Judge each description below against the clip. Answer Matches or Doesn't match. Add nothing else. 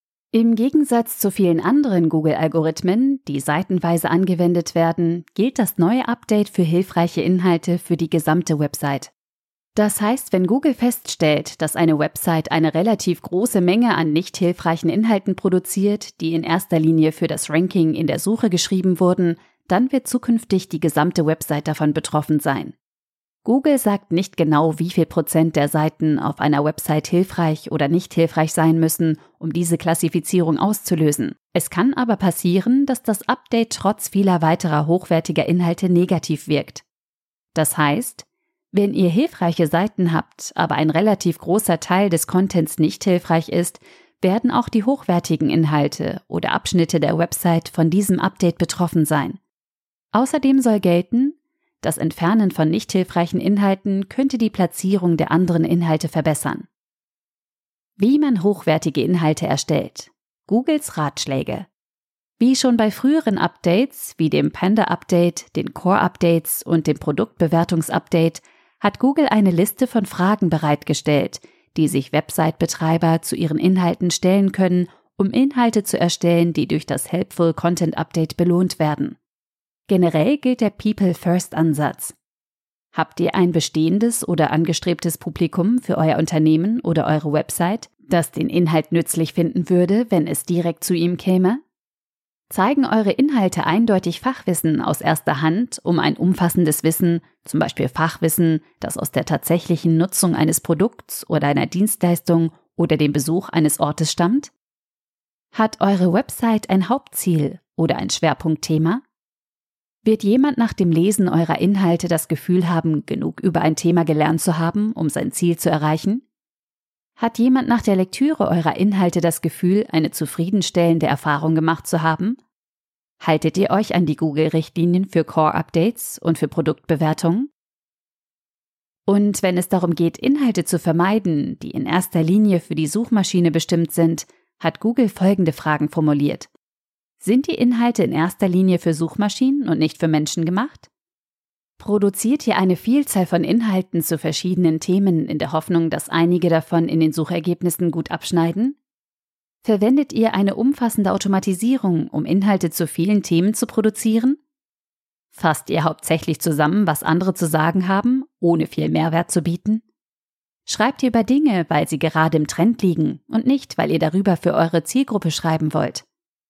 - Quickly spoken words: Doesn't match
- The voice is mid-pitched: Matches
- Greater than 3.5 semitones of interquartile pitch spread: Matches